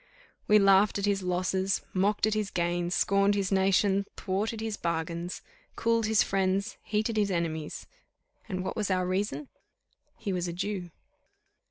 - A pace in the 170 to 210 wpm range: No, average, 155 wpm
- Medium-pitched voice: No, high, 195 Hz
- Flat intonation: Yes, narrow, 2.3 semitones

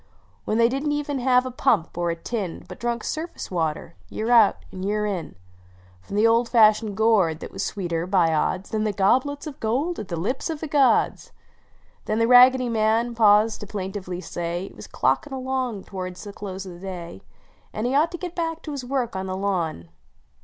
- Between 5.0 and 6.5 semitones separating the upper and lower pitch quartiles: Yes, wide, 5.4 semitones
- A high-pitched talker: Yes, high, 215 Hz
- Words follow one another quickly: Yes, fast, 220 wpm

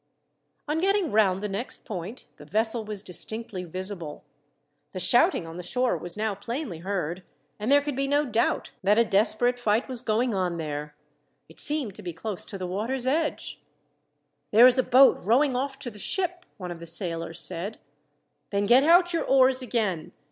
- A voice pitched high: Yes, high, 215 Hz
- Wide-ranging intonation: Yes, wide, 6.0 semitones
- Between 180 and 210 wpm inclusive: Yes, average, 185 wpm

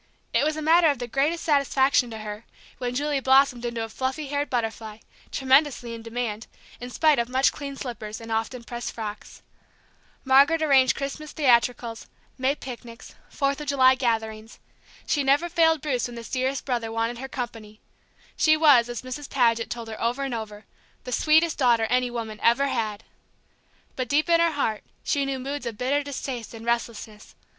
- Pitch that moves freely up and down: No, average, 3.4 semitones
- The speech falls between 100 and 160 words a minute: No, average, 180 wpm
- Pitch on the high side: Yes, very high, 250 Hz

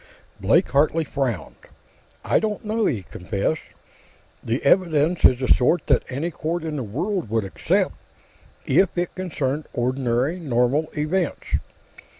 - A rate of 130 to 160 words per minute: Yes, slow, 135 wpm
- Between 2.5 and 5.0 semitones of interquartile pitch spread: No, wide, 5.6 semitones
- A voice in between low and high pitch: Yes, medium, 150 Hz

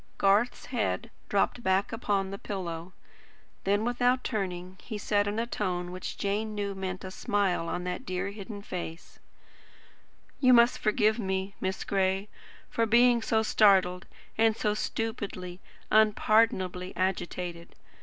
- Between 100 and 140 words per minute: Yes, slow, 135 wpm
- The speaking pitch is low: No, high, 200 Hz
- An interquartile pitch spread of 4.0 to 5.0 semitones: No, average, 3.0 semitones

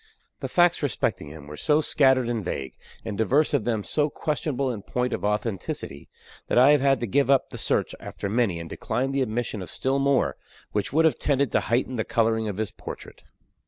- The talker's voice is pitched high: No, low, 120 Hz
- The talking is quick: Yes, fast, 210 wpm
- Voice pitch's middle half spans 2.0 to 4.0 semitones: No, average, 4.8 semitones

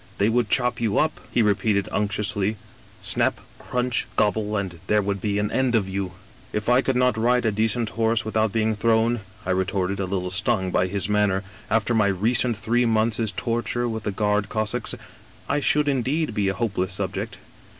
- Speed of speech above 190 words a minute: Yes, average, 200 wpm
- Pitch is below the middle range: Yes, low, 110 Hz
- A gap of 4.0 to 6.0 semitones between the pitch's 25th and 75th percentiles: No, average, 2.8 semitones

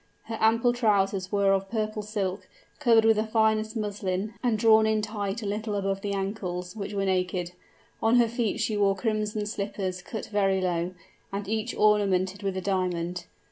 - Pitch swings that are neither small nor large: No, narrow, 2.1 semitones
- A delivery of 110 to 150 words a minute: No, average, 180 wpm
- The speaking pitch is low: No, high, 205 Hz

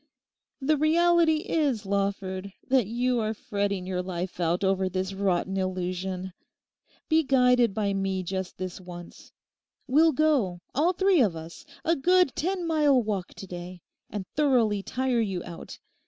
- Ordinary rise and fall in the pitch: No, wide, 7.1 semitones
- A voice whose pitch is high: Yes, high, 200 Hz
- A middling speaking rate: Yes, average, 150 wpm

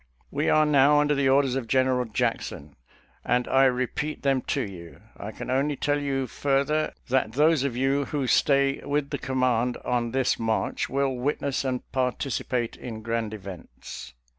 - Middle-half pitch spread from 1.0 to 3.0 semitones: Yes, narrow, 2.4 semitones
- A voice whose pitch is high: No, low, 130 Hz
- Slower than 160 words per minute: No, average, 165 wpm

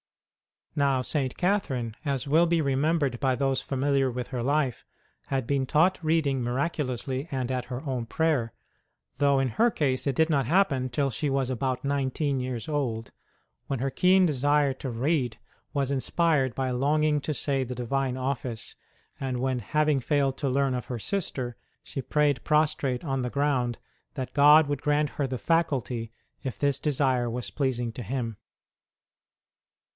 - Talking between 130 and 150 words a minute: No, average, 165 wpm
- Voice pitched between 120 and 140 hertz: Yes, low, 135 Hz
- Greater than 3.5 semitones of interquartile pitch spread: No, average, 2.7 semitones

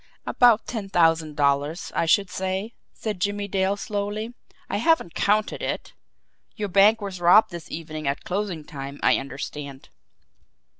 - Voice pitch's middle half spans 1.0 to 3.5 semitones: No, average, 4.9 semitones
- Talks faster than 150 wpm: No, average, 145 wpm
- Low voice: No, high, 190 Hz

